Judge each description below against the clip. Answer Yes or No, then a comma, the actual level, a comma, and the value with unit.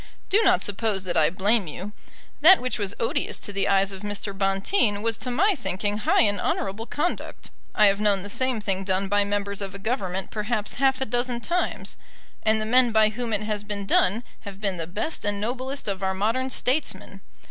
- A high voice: Yes, high, 210 Hz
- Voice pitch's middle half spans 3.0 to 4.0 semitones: Yes, average, 3.6 semitones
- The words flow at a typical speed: No, fast, 210 wpm